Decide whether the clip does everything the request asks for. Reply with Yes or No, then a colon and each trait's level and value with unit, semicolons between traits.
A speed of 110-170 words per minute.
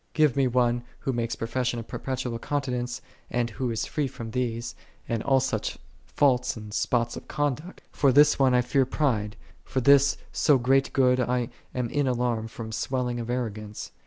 No: average, 185 wpm